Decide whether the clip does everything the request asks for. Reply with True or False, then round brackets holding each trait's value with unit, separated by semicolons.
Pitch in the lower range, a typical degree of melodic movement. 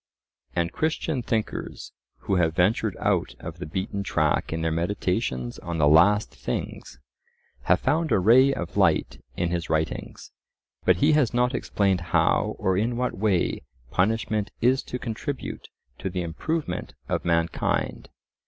False (95 Hz; 6.1 semitones)